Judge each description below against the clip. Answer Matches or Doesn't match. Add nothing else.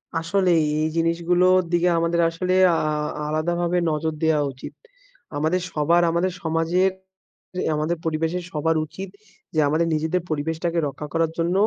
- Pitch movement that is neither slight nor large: Doesn't match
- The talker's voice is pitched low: Doesn't match